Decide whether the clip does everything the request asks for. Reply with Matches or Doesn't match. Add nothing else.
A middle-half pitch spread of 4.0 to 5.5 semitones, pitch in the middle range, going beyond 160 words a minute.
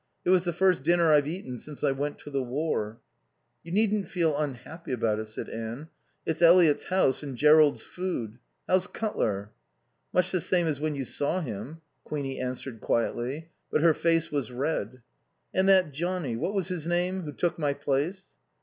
Matches